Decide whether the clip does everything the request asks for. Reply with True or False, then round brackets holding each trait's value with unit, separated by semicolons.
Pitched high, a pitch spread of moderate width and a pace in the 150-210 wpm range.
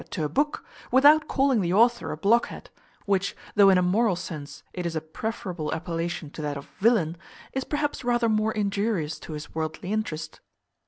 False (195 Hz; 6.2 semitones; 180 wpm)